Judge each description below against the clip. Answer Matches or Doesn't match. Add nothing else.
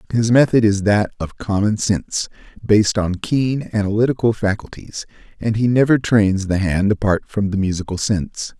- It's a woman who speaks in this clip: Doesn't match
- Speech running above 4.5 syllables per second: Matches